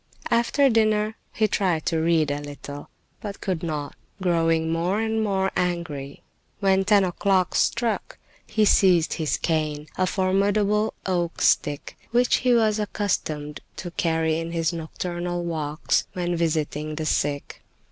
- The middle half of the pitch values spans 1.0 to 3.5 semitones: No, average, 4.3 semitones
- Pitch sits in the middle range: Yes, medium, 175 Hz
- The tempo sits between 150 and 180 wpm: No, average, 140 wpm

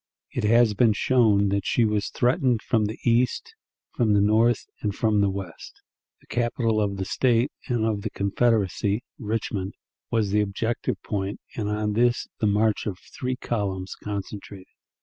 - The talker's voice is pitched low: Yes, low, 105 Hz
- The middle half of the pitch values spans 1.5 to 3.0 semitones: Yes, narrow, 2.6 semitones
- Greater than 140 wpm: Yes, average, 165 wpm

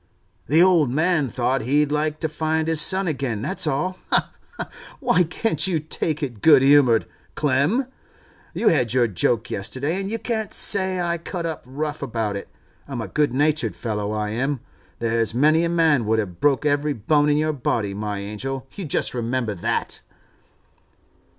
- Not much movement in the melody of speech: No, average, 5.2 semitones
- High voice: No, medium, 145 Hz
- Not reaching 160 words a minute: No, average, 175 wpm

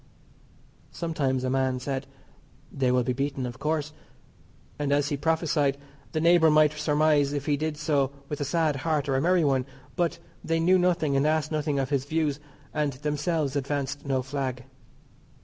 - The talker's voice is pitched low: No, medium, 145 Hz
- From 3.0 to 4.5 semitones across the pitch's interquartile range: No, narrow, 2.4 semitones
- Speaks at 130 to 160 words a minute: No, average, 175 wpm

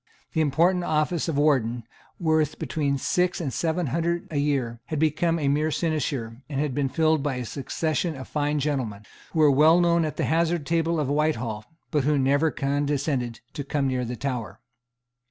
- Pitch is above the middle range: No, medium, 150 Hz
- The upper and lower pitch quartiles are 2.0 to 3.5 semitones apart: Yes, average, 2.9 semitones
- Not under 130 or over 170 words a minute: No, average, 185 wpm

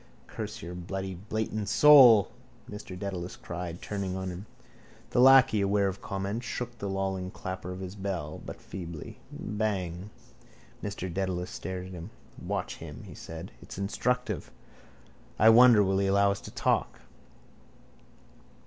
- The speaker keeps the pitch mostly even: Yes, narrow, 2.3 semitones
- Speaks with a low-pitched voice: Yes, very low, 95 Hz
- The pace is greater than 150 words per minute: No, average, 145 wpm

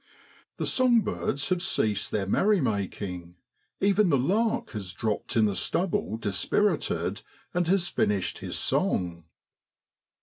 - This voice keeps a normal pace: No, slow, 125 wpm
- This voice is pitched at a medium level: No, low, 115 Hz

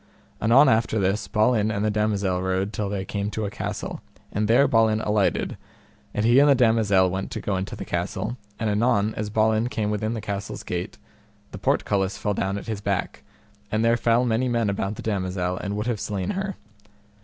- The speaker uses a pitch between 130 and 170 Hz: No, low, 105 Hz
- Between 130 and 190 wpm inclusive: No, average, 200 wpm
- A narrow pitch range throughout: Yes, narrow, 2.2 semitones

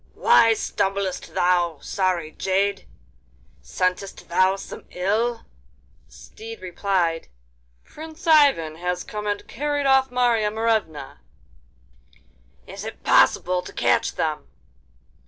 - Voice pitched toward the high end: Yes, high, 195 Hz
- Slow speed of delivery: Yes, slow, 105 wpm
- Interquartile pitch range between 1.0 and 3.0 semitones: No, average, 4.3 semitones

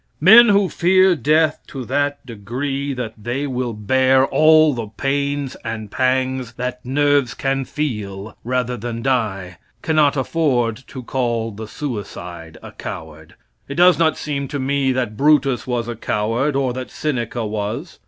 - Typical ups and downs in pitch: Yes, average, 3.8 semitones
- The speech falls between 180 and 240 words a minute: No, average, 155 wpm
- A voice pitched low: Yes, low, 130 Hz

